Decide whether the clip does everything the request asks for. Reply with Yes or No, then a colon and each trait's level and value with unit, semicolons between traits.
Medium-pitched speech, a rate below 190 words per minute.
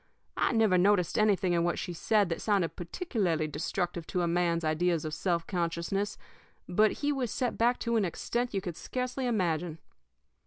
Yes: medium, 180 Hz; average, 180 wpm